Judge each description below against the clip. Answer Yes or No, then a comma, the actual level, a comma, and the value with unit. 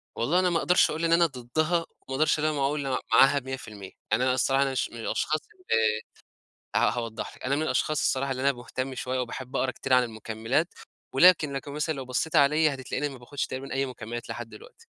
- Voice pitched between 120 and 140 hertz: Yes, low, 135 Hz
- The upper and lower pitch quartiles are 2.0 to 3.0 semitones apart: No, average, 3.7 semitones